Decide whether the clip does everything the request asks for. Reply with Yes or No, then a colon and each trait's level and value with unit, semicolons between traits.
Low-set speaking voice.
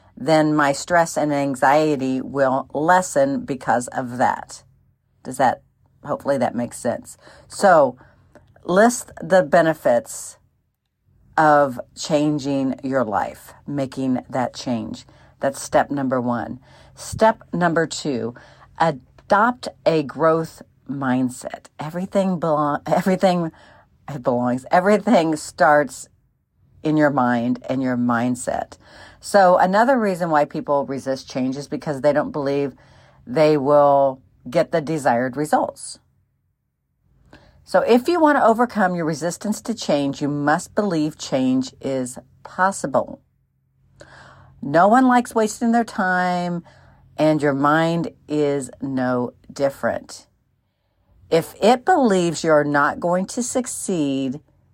No: medium, 150 Hz